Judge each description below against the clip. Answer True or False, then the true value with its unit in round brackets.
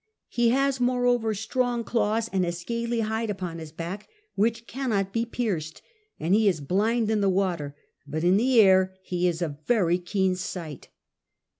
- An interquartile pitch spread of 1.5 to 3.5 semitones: False (4.7 semitones)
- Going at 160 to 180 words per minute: True (175 wpm)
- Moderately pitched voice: False (200 Hz)